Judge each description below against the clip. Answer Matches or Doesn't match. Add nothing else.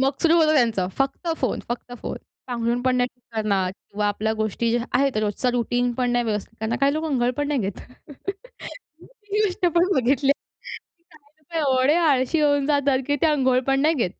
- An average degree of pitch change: Matches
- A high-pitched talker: Matches